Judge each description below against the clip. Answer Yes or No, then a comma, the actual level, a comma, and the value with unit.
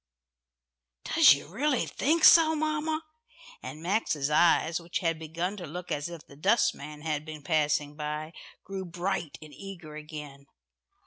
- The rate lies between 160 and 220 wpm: No, average, 145 wpm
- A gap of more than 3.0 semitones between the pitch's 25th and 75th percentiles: Yes, average, 4.5 semitones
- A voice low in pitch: No, medium, 165 Hz